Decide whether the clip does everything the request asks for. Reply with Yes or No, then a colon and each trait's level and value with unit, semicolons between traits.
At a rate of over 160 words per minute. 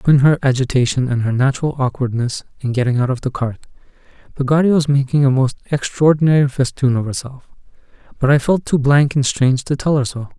Yes: average, 190 wpm